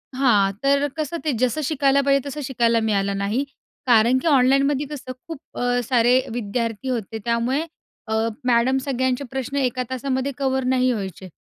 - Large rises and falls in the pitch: No, average, 2.8 semitones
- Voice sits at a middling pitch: No, very high, 255 Hz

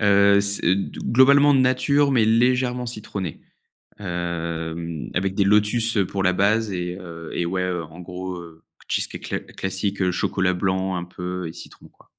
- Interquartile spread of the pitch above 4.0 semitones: No, average, 3.6 semitones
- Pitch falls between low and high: No, very low, 95 Hz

